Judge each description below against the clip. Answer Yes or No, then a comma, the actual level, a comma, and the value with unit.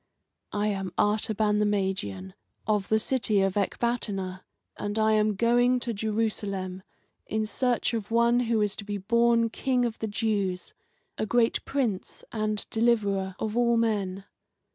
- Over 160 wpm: No, average, 150 wpm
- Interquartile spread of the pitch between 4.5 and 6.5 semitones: No, average, 2.7 semitones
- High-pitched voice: Yes, high, 215 Hz